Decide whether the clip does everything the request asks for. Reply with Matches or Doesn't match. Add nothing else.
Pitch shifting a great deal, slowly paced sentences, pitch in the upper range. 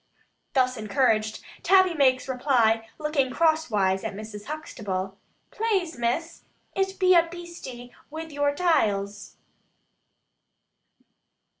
Matches